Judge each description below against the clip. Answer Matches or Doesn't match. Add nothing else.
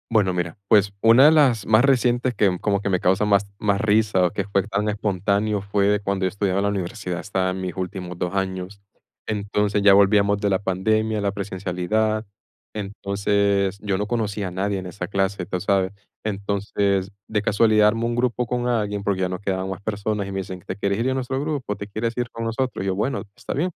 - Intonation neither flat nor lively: Doesn't match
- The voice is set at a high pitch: Doesn't match